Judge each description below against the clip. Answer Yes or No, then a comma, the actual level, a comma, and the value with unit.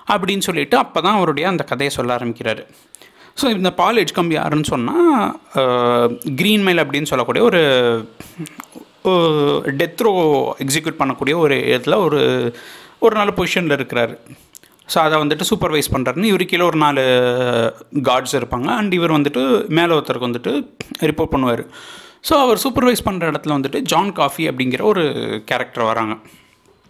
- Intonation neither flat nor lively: No, wide, 6.7 semitones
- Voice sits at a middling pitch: Yes, medium, 155 Hz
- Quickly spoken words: Yes, fast, 135 wpm